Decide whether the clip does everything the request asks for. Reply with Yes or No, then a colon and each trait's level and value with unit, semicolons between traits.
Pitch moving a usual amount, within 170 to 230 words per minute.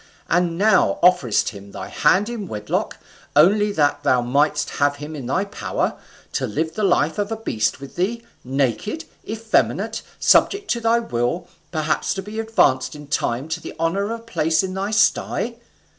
No: wide, 6.8 semitones; average, 175 wpm